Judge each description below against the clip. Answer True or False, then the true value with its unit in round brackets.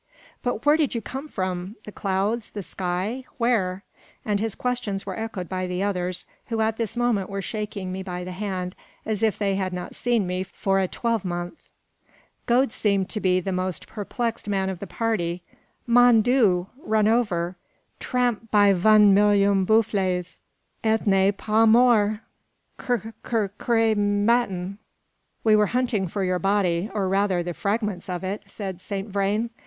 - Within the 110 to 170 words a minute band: True (165 wpm)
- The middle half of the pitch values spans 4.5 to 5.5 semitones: False (3.2 semitones)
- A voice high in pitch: True (205 Hz)